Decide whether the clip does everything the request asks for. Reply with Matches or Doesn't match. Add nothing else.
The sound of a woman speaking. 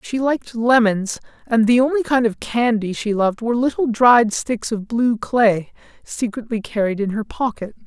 Doesn't match